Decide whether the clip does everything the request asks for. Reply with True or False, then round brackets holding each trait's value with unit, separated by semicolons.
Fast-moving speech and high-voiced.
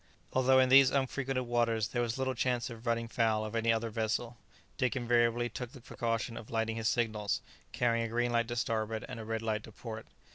False (215 wpm; 115 Hz)